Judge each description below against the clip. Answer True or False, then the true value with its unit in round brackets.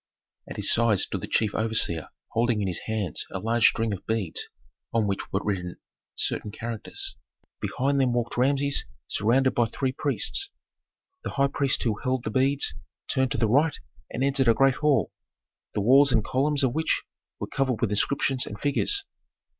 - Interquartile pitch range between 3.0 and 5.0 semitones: True (3.9 semitones)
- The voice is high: False (120 Hz)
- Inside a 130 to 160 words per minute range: False (180 wpm)